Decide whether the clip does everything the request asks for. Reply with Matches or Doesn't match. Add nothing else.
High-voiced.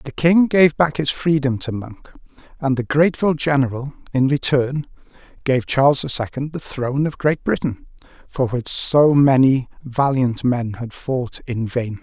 Doesn't match